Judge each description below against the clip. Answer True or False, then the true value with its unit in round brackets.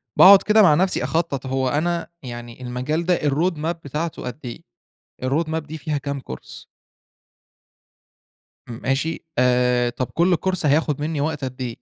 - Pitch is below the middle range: False (150 Hz)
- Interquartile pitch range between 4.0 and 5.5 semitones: True (4.5 semitones)